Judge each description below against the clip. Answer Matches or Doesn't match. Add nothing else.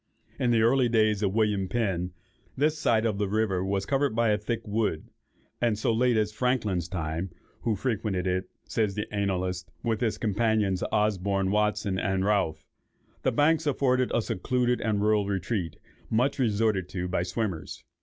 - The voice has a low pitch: Matches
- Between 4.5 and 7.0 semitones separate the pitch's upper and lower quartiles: Doesn't match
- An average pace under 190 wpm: Matches